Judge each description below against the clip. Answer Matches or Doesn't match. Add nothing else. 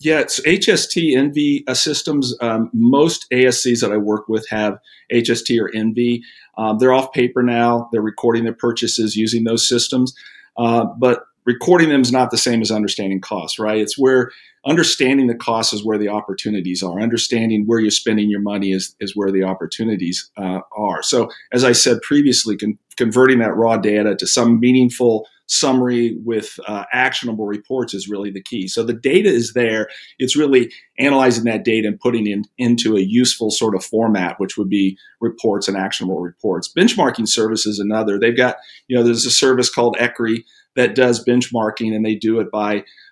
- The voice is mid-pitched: Doesn't match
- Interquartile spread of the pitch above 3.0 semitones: Doesn't match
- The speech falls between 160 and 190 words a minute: Matches